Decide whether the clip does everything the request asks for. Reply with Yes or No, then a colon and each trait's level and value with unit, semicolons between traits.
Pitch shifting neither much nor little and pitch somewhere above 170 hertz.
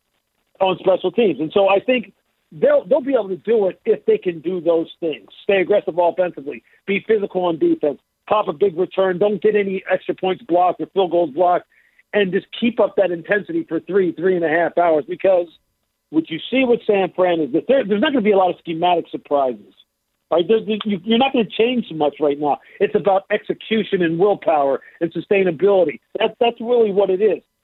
Yes: average, 3.8 semitones; high, 190 Hz